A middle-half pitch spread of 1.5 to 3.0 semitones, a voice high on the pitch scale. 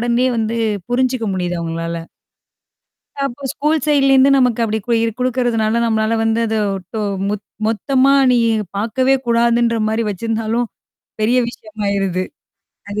Yes: average, 2.7 semitones; high, 230 Hz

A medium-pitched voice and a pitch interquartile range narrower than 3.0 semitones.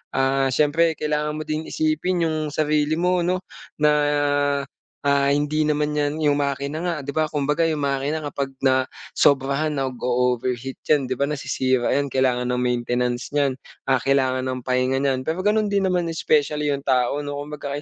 Yes: medium, 145 Hz; narrow, 2.5 semitones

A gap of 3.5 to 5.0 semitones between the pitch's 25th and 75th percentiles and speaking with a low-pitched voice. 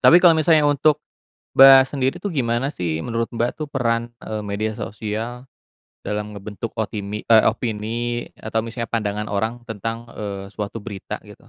No: average, 2.9 semitones; low, 115 Hz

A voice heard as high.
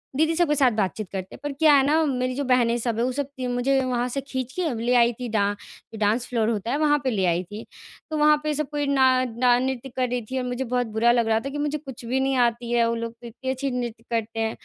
Yes: very high, 250 Hz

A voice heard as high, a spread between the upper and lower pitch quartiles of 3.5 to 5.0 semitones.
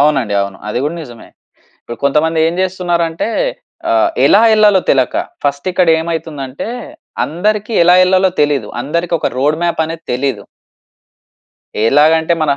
No: medium, 160 Hz; average, 4.1 semitones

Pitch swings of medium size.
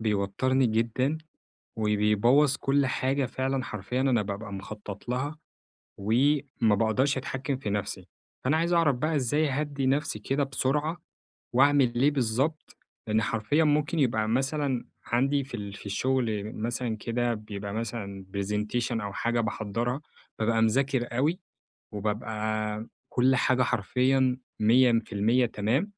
Yes: average, 4.1 semitones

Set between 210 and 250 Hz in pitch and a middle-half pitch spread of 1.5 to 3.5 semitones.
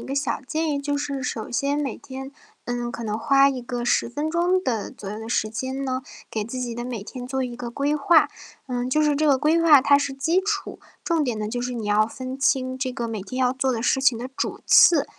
No: very high, 260 Hz; average, 3.1 semitones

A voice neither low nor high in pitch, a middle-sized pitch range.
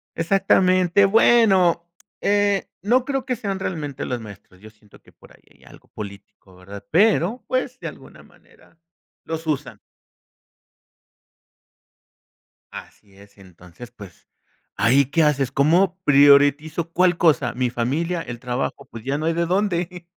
No: medium, 160 Hz; wide, 7.3 semitones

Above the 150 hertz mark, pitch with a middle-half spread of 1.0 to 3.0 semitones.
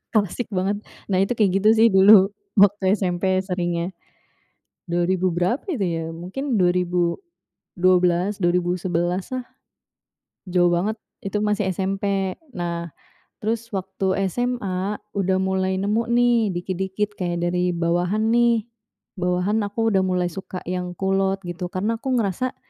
Yes: high, 190 Hz; average, 2.7 semitones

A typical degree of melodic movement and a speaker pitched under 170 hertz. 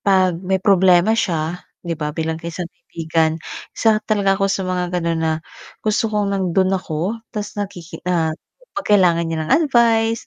No: average, 3.7 semitones; medium, 185 Hz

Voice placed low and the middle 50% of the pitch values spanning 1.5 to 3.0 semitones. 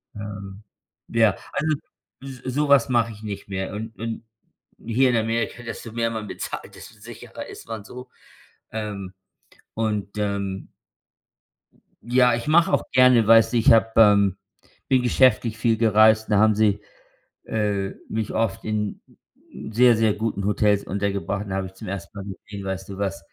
Yes: low, 110 Hz; narrow, 2.4 semitones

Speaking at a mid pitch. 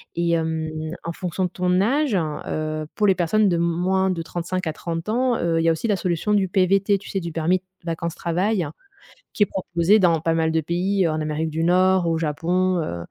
Yes: medium, 175 Hz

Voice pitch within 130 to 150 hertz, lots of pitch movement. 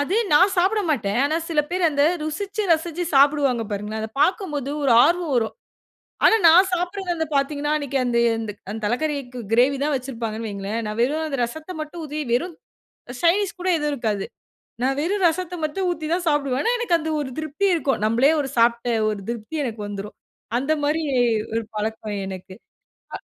No: very high, 290 Hz; wide, 6.1 semitones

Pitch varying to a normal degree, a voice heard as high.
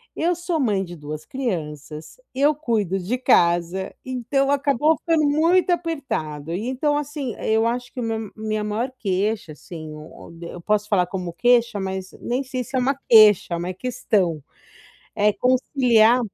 No: wide, 6.4 semitones; high, 225 Hz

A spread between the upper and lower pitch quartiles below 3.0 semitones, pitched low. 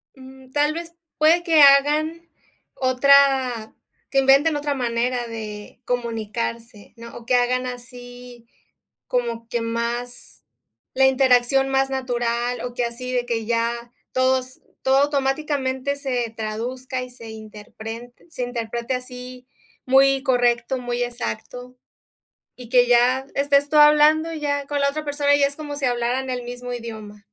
No: narrow, 2.5 semitones; very high, 250 Hz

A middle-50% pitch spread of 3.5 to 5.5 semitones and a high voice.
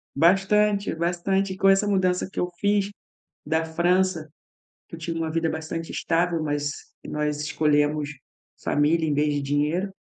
No: average, 3.9 semitones; medium, 165 Hz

